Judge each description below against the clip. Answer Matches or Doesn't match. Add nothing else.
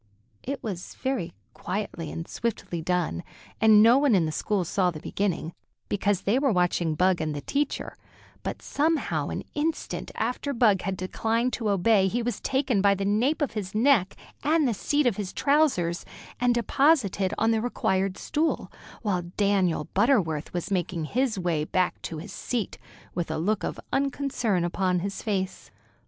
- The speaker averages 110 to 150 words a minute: Doesn't match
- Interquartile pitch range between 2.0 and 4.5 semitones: Doesn't match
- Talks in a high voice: Matches